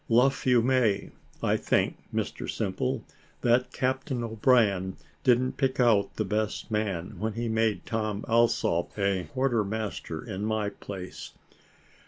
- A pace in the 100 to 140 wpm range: Yes, slow, 135 wpm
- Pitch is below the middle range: Yes, low, 110 Hz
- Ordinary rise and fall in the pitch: Yes, average, 3.3 semitones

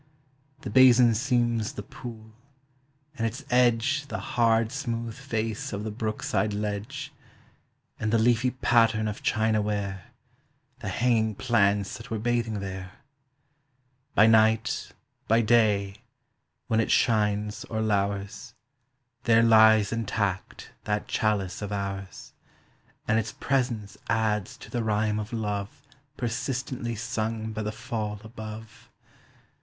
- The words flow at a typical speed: No, slow, 125 wpm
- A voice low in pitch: Yes, low, 110 Hz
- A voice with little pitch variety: Yes, narrow, 2.0 semitones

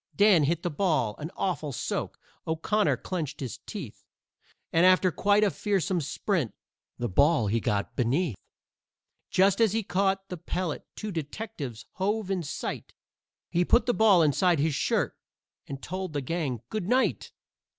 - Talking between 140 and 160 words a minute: Yes, average, 155 wpm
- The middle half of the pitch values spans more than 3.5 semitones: Yes, average, 5.3 semitones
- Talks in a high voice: No, medium, 175 Hz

